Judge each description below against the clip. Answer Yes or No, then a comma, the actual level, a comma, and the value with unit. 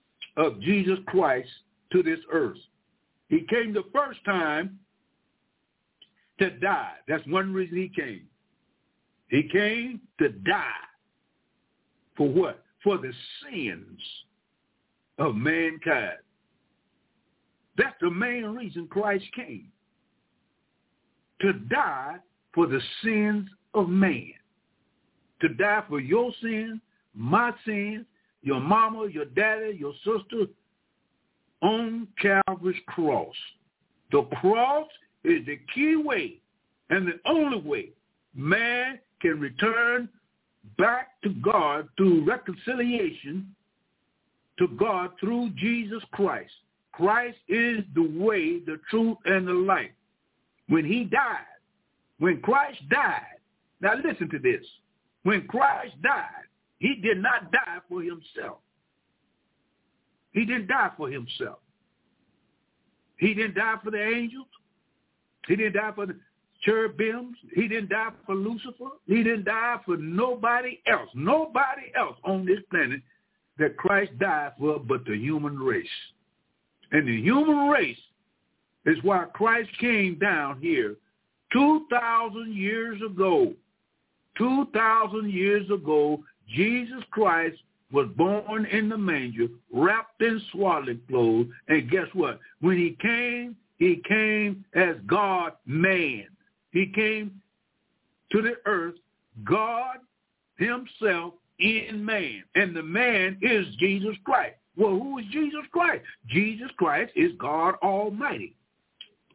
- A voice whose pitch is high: Yes, high, 215 Hz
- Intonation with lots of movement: No, average, 4.3 semitones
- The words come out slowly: Yes, slow, 115 wpm